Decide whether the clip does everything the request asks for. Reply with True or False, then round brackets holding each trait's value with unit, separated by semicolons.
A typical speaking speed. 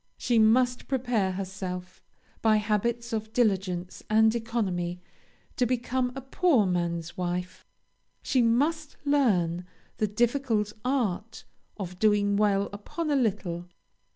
False (120 wpm)